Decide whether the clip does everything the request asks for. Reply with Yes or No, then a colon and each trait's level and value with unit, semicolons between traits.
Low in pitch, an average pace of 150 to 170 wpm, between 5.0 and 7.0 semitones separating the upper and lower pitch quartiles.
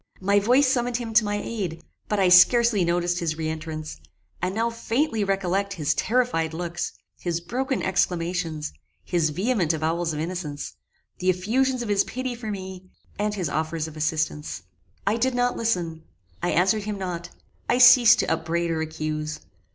No: medium, 180 Hz; average, 165 wpm; wide, 5.5 semitones